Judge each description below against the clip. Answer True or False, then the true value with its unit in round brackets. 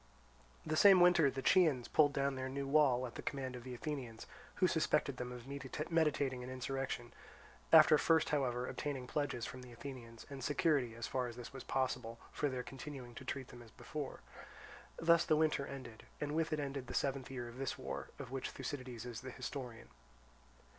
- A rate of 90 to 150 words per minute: False (195 wpm)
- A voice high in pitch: False (135 Hz)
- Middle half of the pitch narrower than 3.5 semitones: True (2.9 semitones)